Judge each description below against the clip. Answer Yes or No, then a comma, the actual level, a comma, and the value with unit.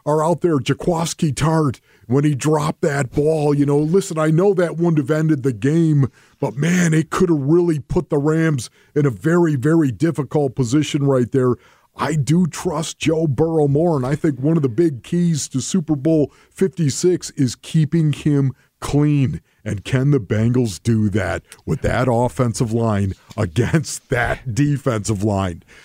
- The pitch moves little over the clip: No, average, 3.7 semitones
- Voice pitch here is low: No, medium, 150 Hz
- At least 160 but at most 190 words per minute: Yes, average, 170 wpm